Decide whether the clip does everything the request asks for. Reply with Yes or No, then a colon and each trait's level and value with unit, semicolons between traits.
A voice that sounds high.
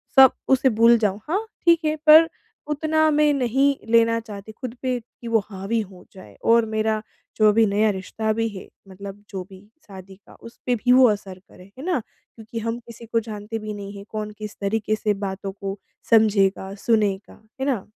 Yes: high, 220 Hz